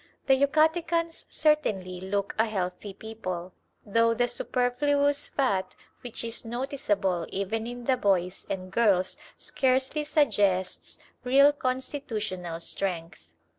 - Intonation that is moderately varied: No, wide, 6.2 semitones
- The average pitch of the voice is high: Yes, high, 230 Hz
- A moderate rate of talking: No, slow, 110 wpm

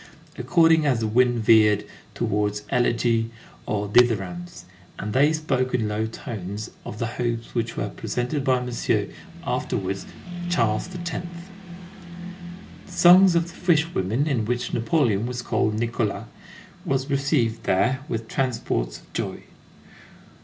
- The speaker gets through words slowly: Yes, slow, 130 wpm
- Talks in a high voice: No, low, 120 Hz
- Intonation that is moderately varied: Yes, average, 4.4 semitones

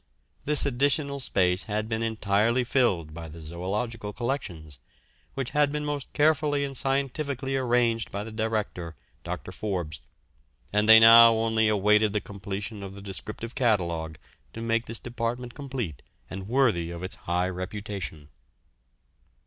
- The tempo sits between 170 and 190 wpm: No, average, 140 wpm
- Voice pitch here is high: No, low, 110 Hz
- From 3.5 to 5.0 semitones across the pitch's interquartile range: Yes, average, 4.7 semitones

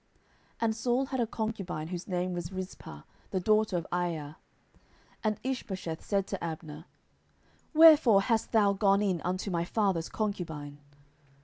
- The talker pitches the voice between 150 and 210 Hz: Yes, high, 190 Hz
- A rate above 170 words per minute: No, average, 145 wpm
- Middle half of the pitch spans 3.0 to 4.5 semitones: Yes, average, 4.0 semitones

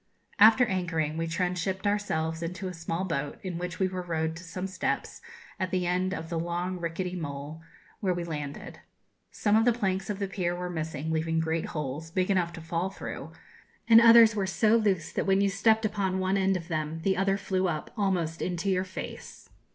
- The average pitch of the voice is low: No, medium, 180 Hz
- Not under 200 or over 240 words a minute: Yes, fast, 205 wpm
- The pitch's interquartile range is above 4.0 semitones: No, average, 2.9 semitones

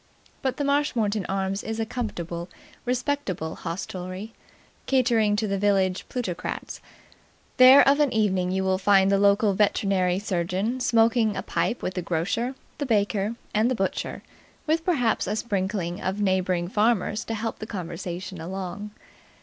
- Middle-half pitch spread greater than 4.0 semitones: No, average, 3.6 semitones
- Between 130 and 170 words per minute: Yes, average, 150 wpm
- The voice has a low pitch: No, high, 205 Hz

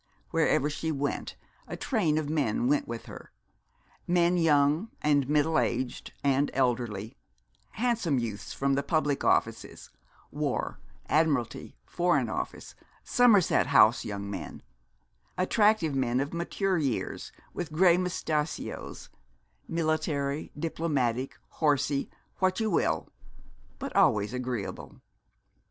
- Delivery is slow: Yes, slow, 110 wpm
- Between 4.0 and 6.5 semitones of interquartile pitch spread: Yes, average, 4.6 semitones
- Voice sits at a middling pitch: Yes, medium, 150 Hz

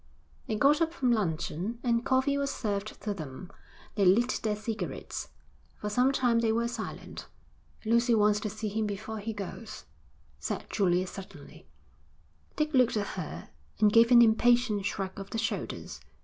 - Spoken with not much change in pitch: No, average, 3.0 semitones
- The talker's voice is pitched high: Yes, high, 220 Hz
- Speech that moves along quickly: No, average, 165 wpm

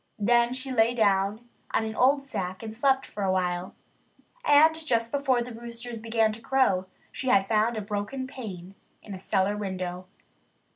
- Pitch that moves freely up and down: No, average, 4.3 semitones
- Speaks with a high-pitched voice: Yes, high, 225 Hz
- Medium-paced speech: Yes, average, 175 wpm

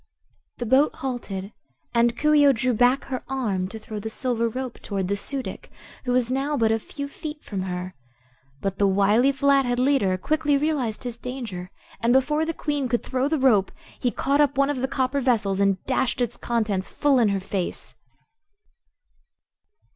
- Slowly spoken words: No, average, 185 wpm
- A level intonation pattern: No, average, 4.7 semitones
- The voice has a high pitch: Yes, high, 245 Hz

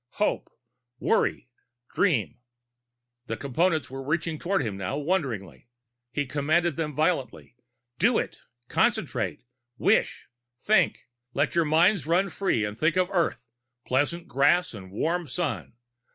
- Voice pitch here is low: No, medium, 155 Hz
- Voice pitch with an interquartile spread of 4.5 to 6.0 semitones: Yes, wide, 5.4 semitones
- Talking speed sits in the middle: No, slow, 125 wpm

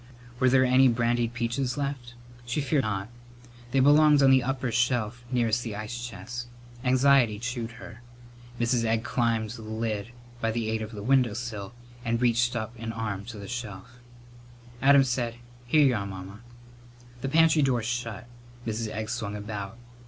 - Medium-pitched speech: No, low, 120 Hz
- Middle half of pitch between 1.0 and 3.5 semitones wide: Yes, narrow, 2.4 semitones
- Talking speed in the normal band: Yes, average, 165 wpm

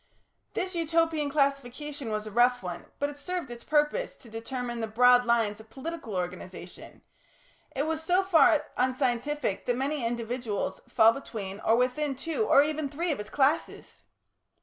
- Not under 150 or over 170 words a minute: Yes, average, 160 wpm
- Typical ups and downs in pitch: Yes, average, 4.8 semitones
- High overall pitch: Yes, very high, 260 Hz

